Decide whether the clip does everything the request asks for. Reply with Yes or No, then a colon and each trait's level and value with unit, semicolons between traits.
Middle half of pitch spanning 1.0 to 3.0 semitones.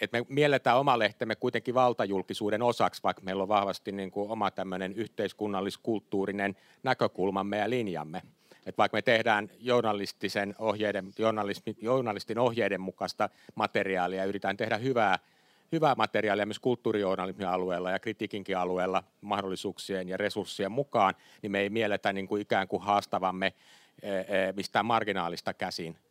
Yes: narrow, 2.6 semitones